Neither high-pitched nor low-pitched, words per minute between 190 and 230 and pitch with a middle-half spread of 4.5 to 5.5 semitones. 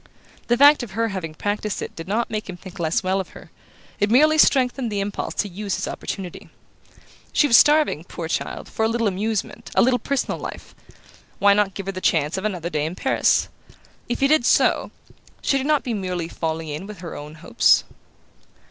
No: high, 205 Hz; fast, 205 wpm; average, 5.1 semitones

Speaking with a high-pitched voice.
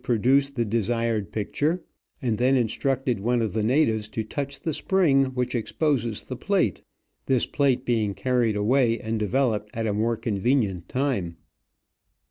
No: low, 120 Hz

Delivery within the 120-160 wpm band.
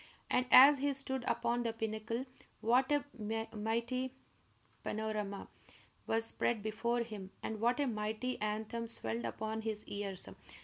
Yes: slow, 135 wpm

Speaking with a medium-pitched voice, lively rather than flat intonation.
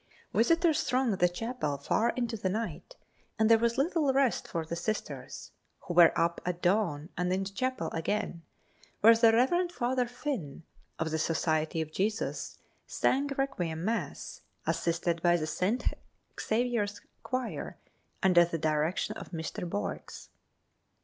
No: high, 205 Hz; wide, 6.5 semitones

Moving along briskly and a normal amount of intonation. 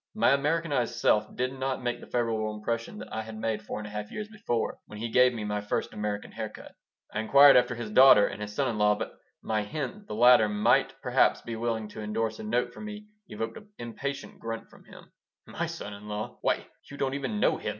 Yes: fast, 230 wpm; average, 3.9 semitones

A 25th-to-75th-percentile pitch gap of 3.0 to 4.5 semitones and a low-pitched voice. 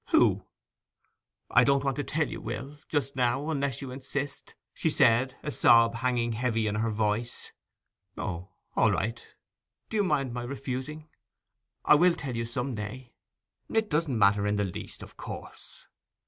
Yes: average, 3.5 semitones; low, 125 Hz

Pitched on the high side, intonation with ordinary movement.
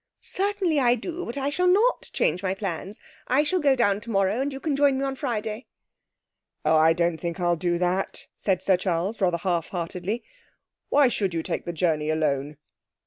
No: high, 195 Hz; wide, 7.7 semitones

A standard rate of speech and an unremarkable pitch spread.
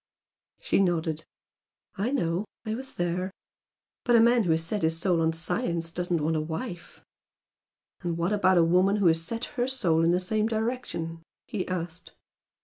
Yes: average, 175 wpm; average, 4.5 semitones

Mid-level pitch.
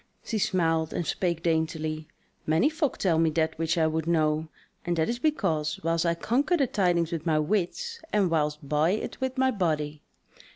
Yes: medium, 165 Hz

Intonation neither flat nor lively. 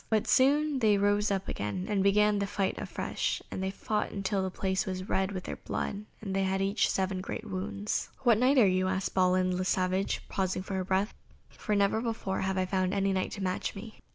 No: narrow, 1.7 semitones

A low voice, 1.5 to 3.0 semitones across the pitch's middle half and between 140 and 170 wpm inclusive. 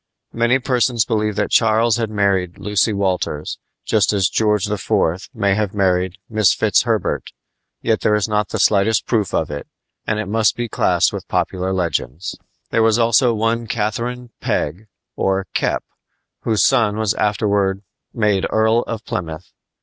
Yes: low, 105 Hz; narrow, 2.6 semitones; average, 155 wpm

